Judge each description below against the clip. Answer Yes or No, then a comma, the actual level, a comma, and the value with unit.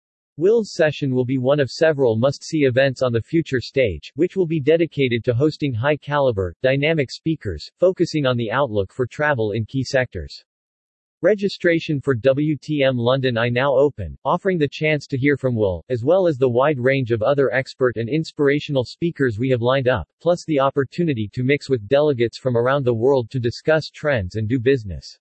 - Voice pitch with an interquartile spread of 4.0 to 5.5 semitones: No, average, 3.4 semitones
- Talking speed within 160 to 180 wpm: No, average, 190 wpm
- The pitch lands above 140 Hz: No, low, 135 Hz